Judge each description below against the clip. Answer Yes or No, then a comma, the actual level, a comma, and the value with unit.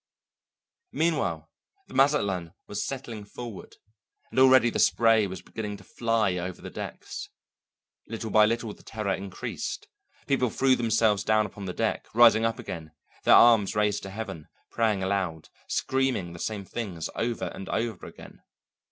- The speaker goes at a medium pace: Yes, average, 150 wpm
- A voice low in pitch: Yes, low, 110 Hz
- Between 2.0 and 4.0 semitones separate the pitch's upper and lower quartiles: Yes, average, 3.2 semitones